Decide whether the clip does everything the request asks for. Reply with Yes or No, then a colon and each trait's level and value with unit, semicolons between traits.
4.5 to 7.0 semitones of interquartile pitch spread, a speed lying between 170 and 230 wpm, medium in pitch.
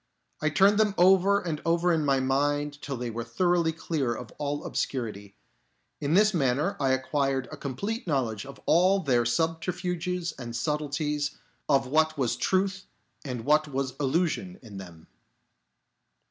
No: average, 4.9 semitones; average, 150 wpm; medium, 145 Hz